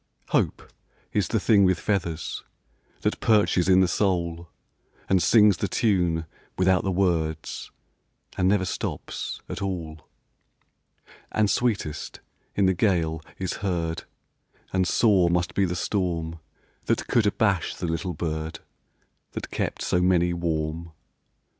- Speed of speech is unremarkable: No, slow, 130 wpm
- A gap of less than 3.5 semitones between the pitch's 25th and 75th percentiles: Yes, average, 2.9 semitones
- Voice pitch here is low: Yes, very low, 90 Hz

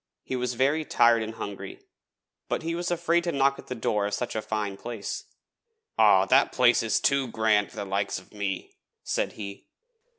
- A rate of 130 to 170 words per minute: No, average, 195 wpm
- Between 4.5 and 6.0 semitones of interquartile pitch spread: Yes, average, 5.2 semitones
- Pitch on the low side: Yes, low, 115 Hz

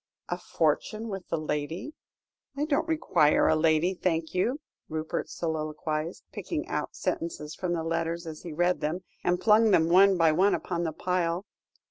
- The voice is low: No, medium, 170 Hz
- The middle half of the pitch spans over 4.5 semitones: No, average, 2.9 semitones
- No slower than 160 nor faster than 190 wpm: Yes, average, 165 wpm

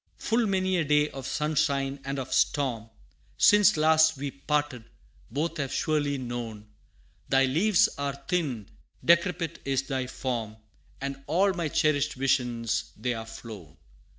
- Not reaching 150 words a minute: Yes, average, 140 wpm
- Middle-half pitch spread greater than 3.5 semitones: Yes, average, 4.0 semitones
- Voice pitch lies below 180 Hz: Yes, medium, 140 Hz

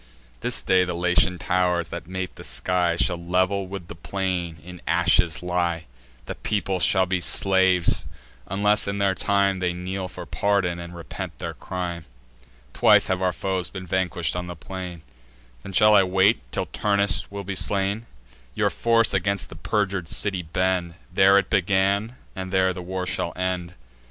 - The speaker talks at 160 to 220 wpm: Yes, average, 165 wpm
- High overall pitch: No, very low, 95 Hz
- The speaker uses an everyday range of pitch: No, narrow, 1.8 semitones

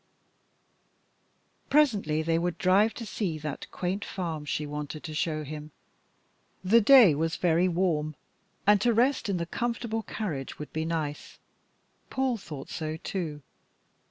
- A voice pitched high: No, medium, 170 Hz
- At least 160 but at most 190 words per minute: No, average, 140 wpm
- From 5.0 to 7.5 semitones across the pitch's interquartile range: Yes, average, 5.3 semitones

